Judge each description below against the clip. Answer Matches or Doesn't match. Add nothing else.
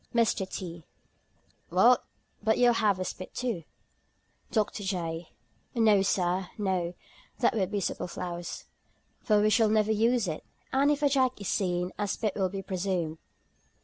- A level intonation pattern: Doesn't match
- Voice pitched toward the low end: Doesn't match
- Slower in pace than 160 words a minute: Matches